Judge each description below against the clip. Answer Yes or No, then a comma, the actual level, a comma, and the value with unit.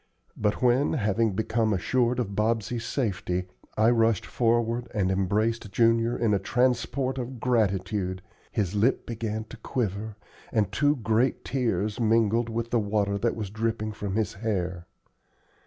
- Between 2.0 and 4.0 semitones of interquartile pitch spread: Yes, average, 2.7 semitones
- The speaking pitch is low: Yes, low, 110 Hz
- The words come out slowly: No, average, 145 wpm